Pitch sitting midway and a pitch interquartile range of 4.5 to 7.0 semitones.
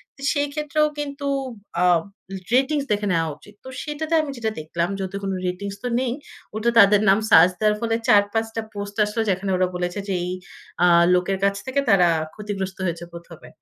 No: high, 205 Hz; wide, 5.4 semitones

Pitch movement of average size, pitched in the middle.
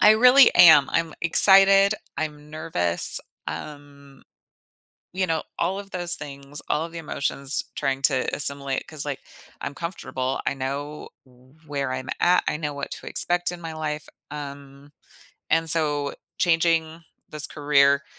Yes: average, 3.1 semitones; medium, 150 Hz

